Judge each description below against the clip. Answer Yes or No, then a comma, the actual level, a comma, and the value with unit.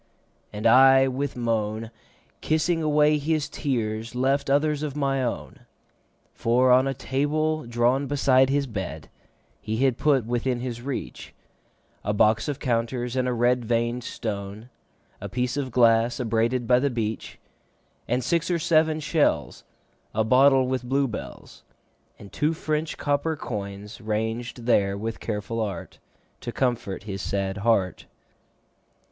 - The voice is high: No, low, 125 Hz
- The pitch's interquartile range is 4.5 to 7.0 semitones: No, average, 3.8 semitones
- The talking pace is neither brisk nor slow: Yes, average, 145 wpm